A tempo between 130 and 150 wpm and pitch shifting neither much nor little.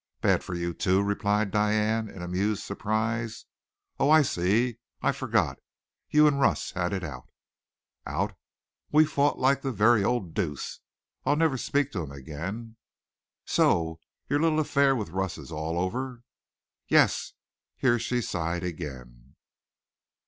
No: average, 140 wpm; wide, 6.4 semitones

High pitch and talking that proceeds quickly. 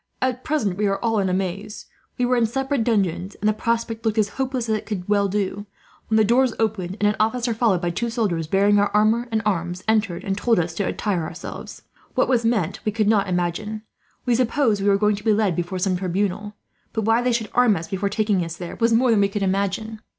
Yes: high, 210 Hz; fast, 240 wpm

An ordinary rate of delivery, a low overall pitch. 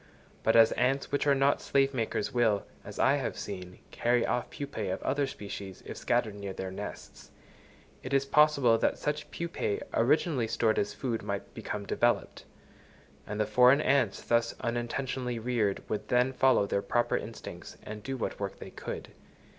Yes: average, 170 wpm; low, 120 Hz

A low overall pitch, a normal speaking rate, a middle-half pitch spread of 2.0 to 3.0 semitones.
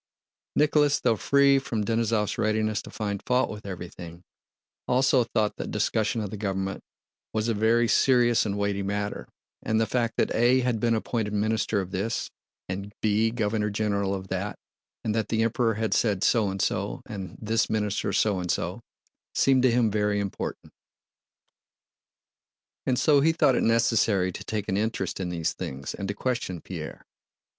Yes: low, 110 Hz; average, 170 wpm; narrow, 2.6 semitones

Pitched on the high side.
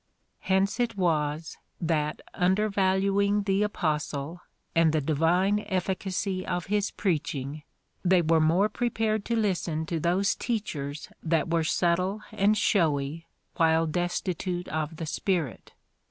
No: medium, 175 Hz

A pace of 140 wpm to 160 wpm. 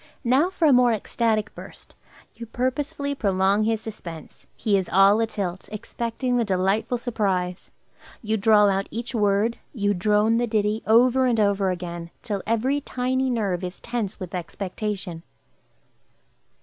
Yes: average, 145 wpm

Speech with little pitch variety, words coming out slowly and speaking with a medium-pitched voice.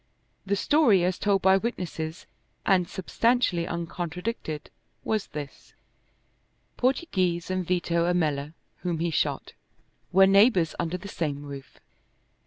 No: average, 3.0 semitones; slow, 115 wpm; medium, 180 Hz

